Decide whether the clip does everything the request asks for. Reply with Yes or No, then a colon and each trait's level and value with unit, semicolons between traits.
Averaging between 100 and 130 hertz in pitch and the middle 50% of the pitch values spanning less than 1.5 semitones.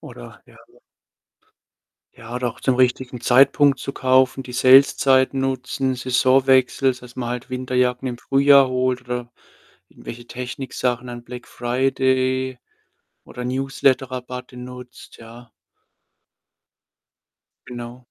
Yes: low, 125 Hz; narrow, 1.1 semitones